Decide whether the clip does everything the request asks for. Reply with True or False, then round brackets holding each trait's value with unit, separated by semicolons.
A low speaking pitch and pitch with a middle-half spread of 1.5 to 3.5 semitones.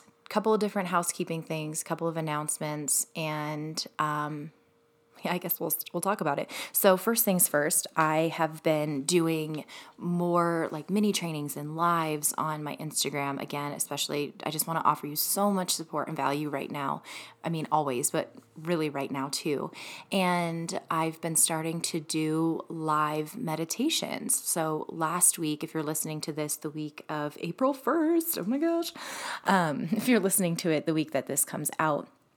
False (160 Hz; 2.5 semitones)